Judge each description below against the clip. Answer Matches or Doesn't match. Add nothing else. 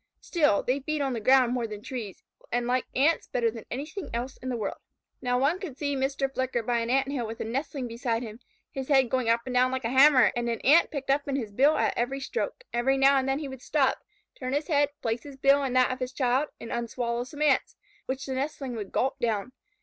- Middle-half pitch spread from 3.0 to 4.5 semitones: Doesn't match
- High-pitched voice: Matches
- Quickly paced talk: Matches